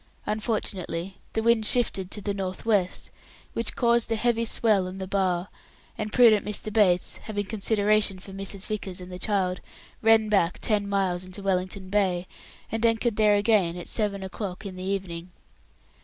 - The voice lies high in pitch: Yes, high, 200 Hz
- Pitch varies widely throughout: No, average, 2.7 semitones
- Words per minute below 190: Yes, average, 170 wpm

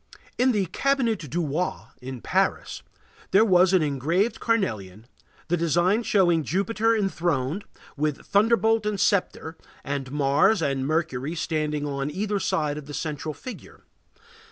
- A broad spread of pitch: Yes, wide, 5.8 semitones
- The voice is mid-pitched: Yes, medium, 170 Hz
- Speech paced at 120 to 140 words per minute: Yes, slow, 135 wpm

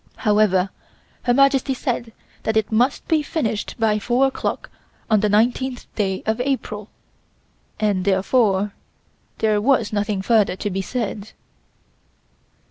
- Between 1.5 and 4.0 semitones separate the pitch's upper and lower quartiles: Yes, average, 3.3 semitones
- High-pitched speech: Yes, high, 220 Hz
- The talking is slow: Yes, slow, 130 wpm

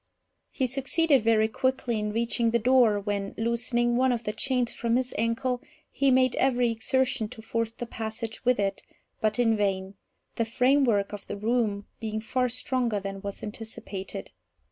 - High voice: Yes, high, 230 Hz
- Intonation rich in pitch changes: No, average, 2.9 semitones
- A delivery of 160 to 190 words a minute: Yes, average, 165 wpm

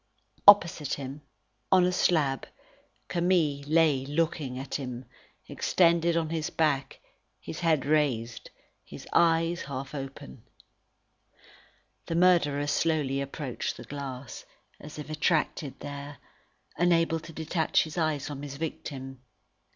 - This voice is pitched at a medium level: Yes, medium, 150 Hz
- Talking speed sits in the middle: No, slow, 120 wpm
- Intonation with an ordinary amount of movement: Yes, average, 3.2 semitones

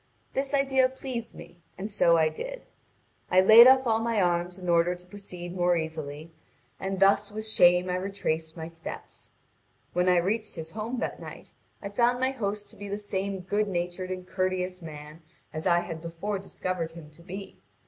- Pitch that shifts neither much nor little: Yes, average, 3.5 semitones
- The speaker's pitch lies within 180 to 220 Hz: Yes, medium, 185 Hz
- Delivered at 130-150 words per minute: No, average, 190 wpm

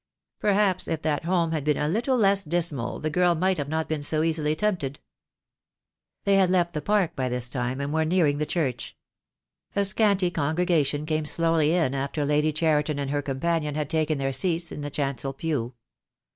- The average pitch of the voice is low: No, medium, 155 Hz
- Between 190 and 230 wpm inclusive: Yes, average, 195 wpm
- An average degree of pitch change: Yes, average, 3.3 semitones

